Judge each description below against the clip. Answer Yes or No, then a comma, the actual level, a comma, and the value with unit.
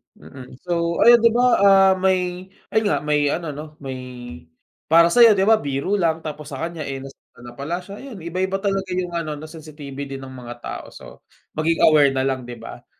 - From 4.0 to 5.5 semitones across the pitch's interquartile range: Yes, average, 5.1 semitones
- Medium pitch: Yes, medium, 160 Hz